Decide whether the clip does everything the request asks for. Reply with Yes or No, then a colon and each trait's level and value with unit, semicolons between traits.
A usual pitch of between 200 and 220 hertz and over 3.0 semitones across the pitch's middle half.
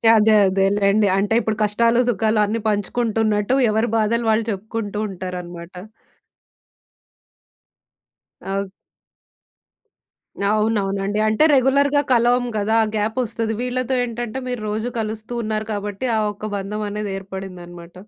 No: high, 215 Hz; narrow, 2.5 semitones